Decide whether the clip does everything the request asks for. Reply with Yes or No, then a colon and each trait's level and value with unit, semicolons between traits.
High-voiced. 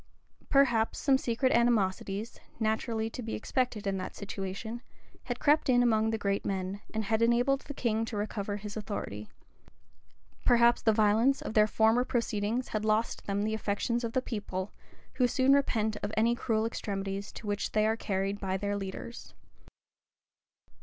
Yes: high, 220 Hz